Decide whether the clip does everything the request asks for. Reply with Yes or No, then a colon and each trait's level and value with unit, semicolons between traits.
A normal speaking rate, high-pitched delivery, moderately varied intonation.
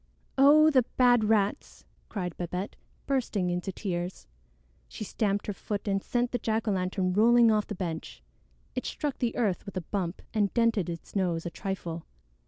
Yes: average, 175 wpm; high, 200 Hz; average, 4.2 semitones